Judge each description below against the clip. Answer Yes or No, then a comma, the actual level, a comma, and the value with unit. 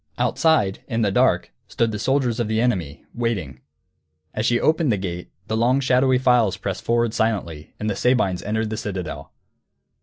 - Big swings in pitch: No, average, 4.1 semitones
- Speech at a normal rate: Yes, average, 175 wpm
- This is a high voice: No, low, 110 Hz